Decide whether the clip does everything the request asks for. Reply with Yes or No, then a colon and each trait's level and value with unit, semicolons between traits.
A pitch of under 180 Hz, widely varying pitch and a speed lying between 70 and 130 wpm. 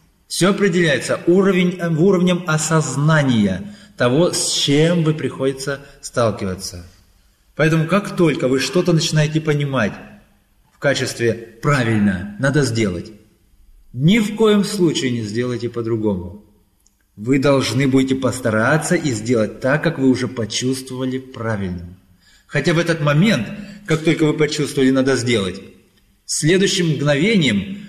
Yes: medium, 140 Hz; wide, 6.6 semitones; average, 115 wpm